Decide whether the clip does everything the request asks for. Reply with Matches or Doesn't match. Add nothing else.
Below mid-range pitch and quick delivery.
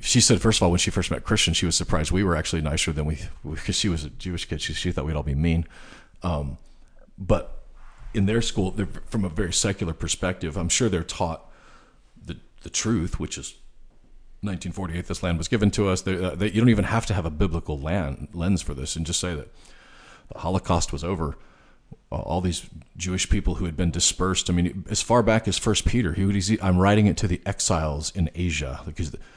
Matches